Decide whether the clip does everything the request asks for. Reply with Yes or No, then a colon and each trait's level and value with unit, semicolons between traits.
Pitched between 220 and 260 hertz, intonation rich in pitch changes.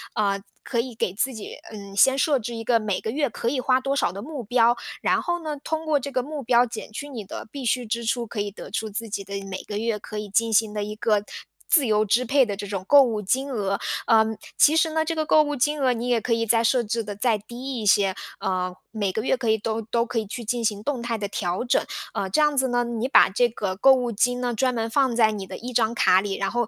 No: high, 230 Hz; average, 3.5 semitones